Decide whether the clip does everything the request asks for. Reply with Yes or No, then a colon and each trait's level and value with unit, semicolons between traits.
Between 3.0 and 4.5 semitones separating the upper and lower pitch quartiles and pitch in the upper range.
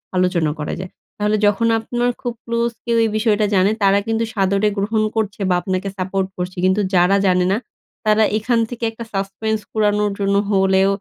No: narrow, 2.5 semitones; high, 205 Hz